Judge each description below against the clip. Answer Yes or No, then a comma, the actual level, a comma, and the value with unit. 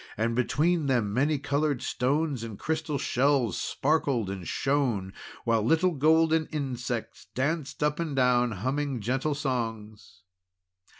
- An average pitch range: Yes, average, 4.4 semitones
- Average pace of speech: No, slow, 125 wpm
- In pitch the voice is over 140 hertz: No, low, 135 Hz